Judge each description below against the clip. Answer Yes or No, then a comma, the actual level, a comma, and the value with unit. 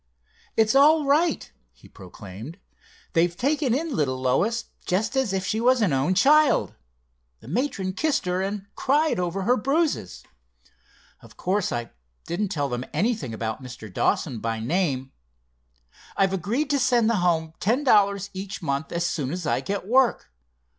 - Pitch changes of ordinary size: No, wide, 8.8 semitones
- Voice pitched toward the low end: No, high, 195 Hz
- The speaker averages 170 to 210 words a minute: No, average, 160 wpm